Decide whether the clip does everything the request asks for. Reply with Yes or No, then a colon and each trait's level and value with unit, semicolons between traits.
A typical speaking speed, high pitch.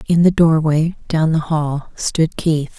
No: average, 170 wpm; medium, 160 Hz